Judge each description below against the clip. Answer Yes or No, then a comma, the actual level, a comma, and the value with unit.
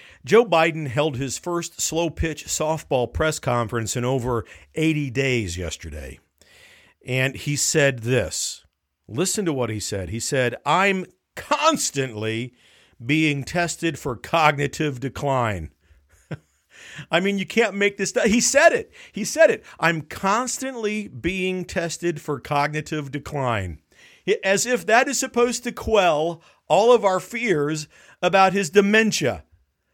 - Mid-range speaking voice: Yes, medium, 155 Hz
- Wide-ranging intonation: Yes, wide, 7.8 semitones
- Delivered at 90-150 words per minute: Yes, slow, 135 wpm